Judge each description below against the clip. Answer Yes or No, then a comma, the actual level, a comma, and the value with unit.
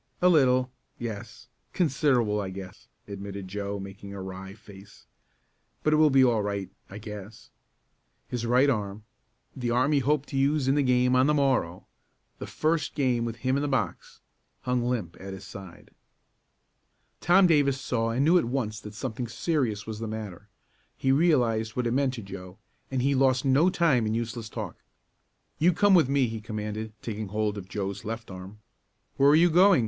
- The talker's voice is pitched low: Yes, low, 120 Hz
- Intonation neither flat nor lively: Yes, average, 4.7 semitones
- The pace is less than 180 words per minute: No, average, 185 wpm